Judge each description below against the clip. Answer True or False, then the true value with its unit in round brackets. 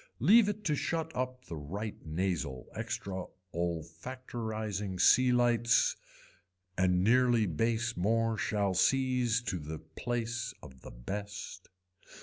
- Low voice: True (110 Hz)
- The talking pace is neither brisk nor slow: False (120 wpm)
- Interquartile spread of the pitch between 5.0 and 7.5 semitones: True (5.3 semitones)